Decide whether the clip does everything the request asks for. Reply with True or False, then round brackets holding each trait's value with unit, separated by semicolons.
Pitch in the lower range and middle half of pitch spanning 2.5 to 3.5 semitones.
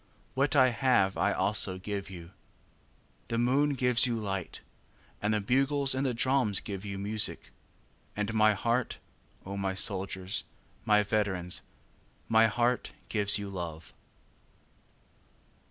False (105 Hz; 4.1 semitones)